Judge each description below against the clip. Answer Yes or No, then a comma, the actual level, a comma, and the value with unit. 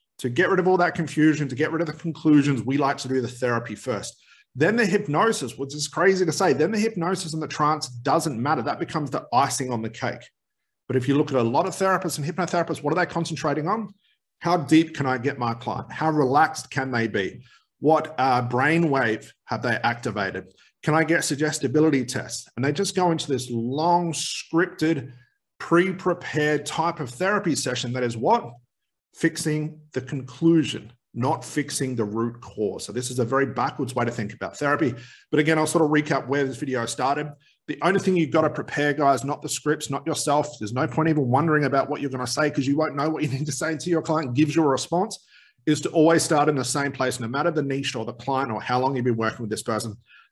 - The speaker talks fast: Yes, fast, 230 wpm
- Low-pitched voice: No, medium, 145 Hz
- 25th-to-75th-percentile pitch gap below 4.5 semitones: Yes, average, 3.9 semitones